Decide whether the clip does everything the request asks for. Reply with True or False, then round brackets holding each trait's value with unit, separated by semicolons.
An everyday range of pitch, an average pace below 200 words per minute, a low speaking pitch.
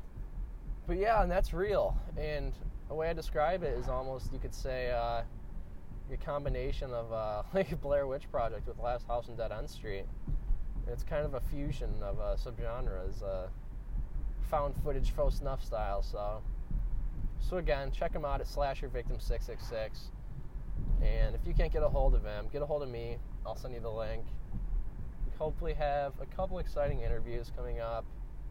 True (3.8 semitones; 175 wpm; 125 Hz)